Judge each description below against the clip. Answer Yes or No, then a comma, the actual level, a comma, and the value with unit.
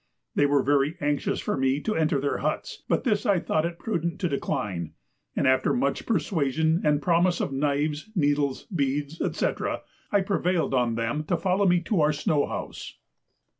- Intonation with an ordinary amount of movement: Yes, average, 3.8 semitones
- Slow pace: No, average, 175 wpm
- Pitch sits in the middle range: Yes, medium, 150 Hz